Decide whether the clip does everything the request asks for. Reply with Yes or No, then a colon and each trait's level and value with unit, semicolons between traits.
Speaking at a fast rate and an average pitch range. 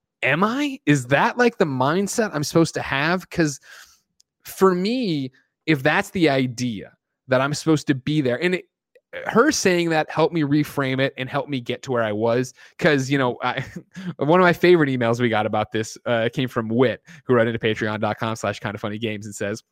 No: fast, 210 wpm; wide, 5.8 semitones